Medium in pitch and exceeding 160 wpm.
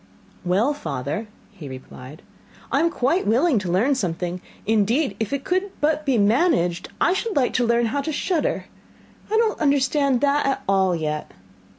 No: very high, 250 Hz; average, 170 wpm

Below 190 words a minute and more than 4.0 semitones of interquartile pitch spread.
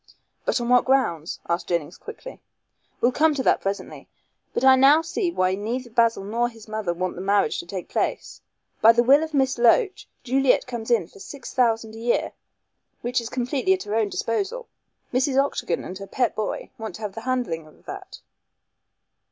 No: average, 195 wpm; average, 4.7 semitones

